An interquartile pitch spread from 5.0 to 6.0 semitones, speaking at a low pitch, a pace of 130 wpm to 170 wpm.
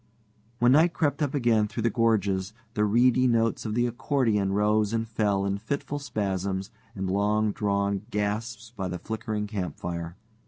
No: average, 2.9 semitones; low, 105 Hz; average, 160 wpm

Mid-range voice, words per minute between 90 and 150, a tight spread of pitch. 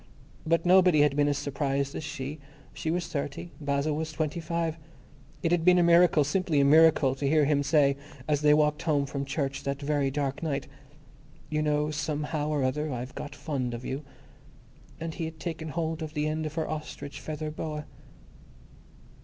No: medium, 150 Hz; average, 185 wpm; narrow, 2.1 semitones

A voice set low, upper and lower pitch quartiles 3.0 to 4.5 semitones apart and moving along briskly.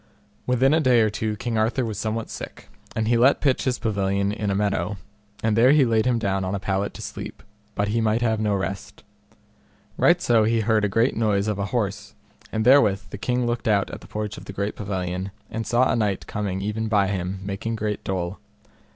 No: low, 105 Hz; narrow, 2.5 semitones; fast, 220 wpm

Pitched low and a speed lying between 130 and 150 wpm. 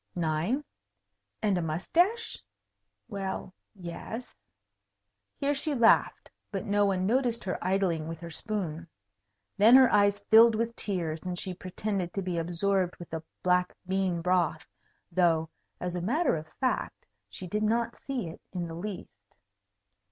No: high, 190 Hz; average, 145 wpm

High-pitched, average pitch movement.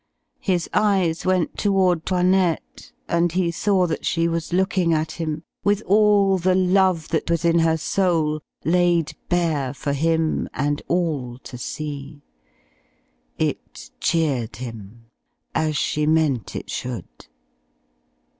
No: medium, 165 Hz; average, 3.3 semitones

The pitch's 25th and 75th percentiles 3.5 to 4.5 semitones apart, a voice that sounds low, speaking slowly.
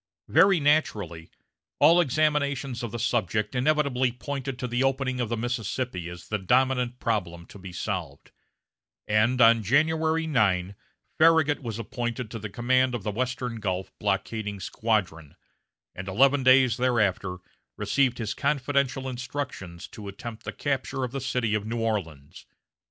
No: average, 4.2 semitones; low, 120 Hz; average, 145 wpm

